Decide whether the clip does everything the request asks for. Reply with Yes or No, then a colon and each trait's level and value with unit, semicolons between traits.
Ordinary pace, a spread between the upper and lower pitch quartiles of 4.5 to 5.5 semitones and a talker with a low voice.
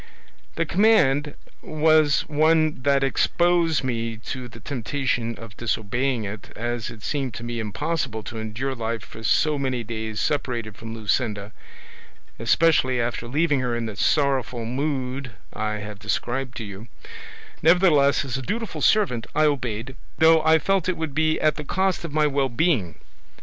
Yes: average, 160 wpm; average, 5.1 semitones; low, 130 Hz